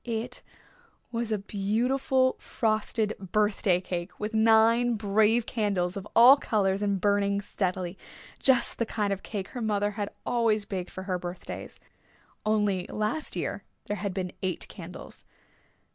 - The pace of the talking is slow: No, average, 145 wpm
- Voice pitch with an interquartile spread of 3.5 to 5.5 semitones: No, narrow, 2.6 semitones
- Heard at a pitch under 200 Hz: No, high, 210 Hz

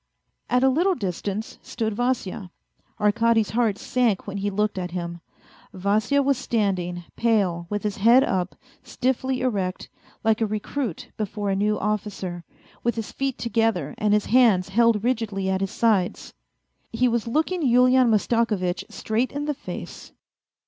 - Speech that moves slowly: No, average, 150 wpm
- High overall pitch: Yes, high, 215 Hz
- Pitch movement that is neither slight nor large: Yes, average, 3.8 semitones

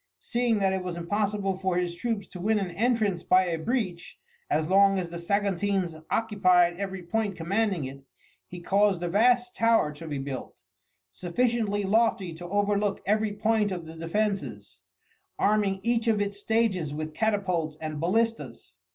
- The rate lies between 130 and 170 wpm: Yes, average, 160 wpm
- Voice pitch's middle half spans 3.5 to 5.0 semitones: Yes, average, 3.8 semitones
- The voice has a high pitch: Yes, high, 195 Hz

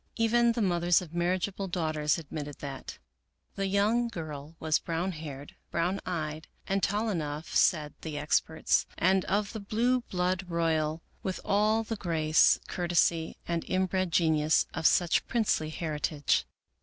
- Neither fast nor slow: Yes, average, 145 wpm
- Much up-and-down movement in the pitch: No, average, 3.9 semitones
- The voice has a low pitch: No, medium, 170 Hz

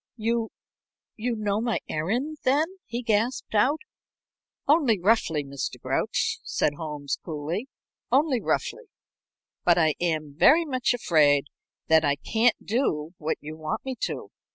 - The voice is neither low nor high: No, high, 210 Hz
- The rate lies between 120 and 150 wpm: Yes, slow, 135 wpm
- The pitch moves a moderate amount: No, wide, 8.1 semitones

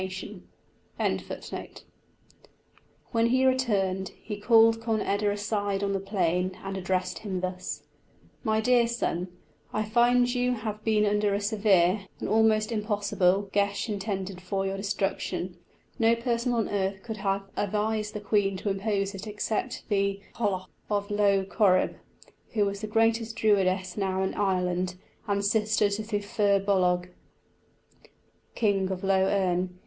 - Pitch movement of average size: No, narrow, 2.2 semitones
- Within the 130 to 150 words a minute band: Yes, average, 140 wpm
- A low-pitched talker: No, high, 205 Hz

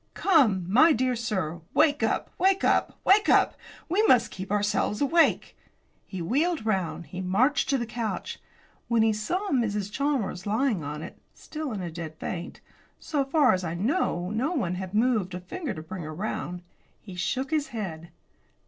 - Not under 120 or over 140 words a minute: No, average, 175 wpm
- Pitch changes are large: Yes, wide, 7.4 semitones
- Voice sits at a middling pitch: No, high, 215 Hz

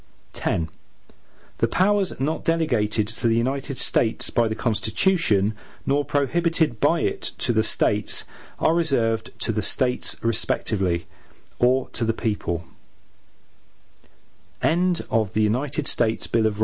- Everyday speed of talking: No, slow, 105 wpm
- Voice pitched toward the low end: Yes, low, 115 Hz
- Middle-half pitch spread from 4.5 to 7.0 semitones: Yes, average, 4.9 semitones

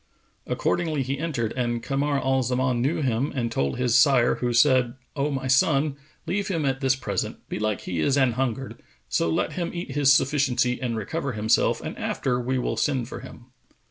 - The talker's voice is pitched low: Yes, low, 130 Hz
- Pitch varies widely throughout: No, narrow, 2.6 semitones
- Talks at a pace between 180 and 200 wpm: Yes, average, 185 wpm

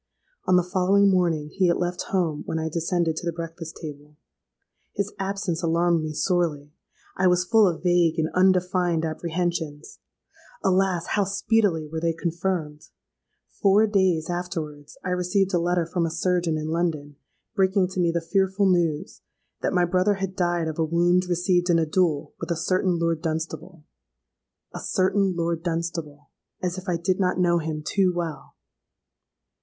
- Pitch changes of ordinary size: No, narrow, 2.2 semitones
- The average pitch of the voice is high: No, medium, 175 Hz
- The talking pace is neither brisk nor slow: Yes, average, 160 wpm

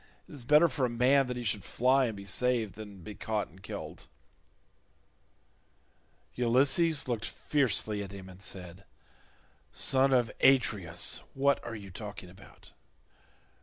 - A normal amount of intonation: Yes, average, 4.7 semitones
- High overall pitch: No, low, 115 Hz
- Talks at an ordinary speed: Yes, average, 145 wpm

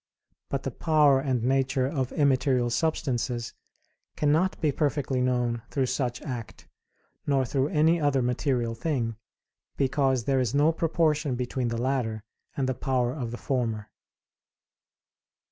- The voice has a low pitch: Yes, low, 130 Hz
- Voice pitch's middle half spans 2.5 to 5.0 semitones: Yes, average, 2.9 semitones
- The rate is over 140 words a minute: No, slow, 135 wpm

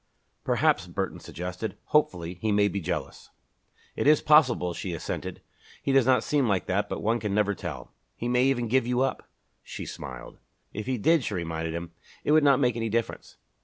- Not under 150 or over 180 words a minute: No, average, 195 wpm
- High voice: No, low, 115 Hz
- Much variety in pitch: Yes, wide, 5.7 semitones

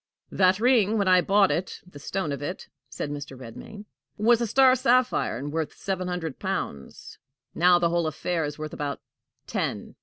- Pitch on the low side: No, medium, 180 Hz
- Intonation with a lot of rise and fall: Yes, wide, 5.8 semitones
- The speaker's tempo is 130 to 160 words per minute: No, average, 180 wpm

